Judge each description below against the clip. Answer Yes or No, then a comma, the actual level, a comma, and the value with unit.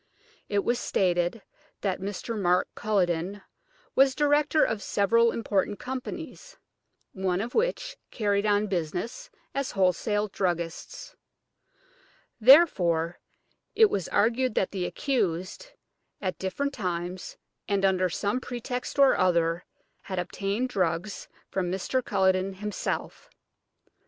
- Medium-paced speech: No, slow, 110 wpm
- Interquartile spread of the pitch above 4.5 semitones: Yes, average, 5.1 semitones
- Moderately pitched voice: No, high, 200 Hz